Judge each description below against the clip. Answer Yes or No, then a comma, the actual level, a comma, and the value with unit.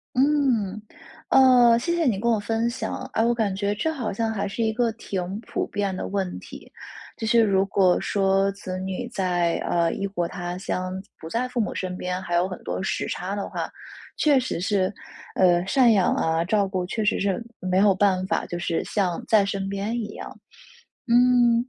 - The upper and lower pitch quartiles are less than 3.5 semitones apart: No, average, 3.8 semitones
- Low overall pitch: No, high, 200 Hz